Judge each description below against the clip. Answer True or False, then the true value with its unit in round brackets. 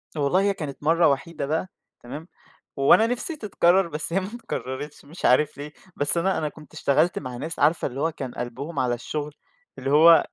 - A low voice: False (150 Hz)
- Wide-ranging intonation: False (3.3 semitones)